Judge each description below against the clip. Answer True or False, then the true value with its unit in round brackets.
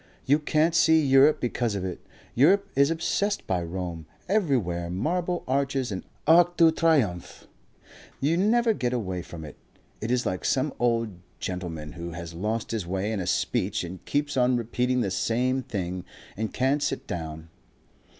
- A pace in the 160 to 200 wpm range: True (165 wpm)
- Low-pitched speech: True (120 Hz)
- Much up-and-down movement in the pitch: True (8.3 semitones)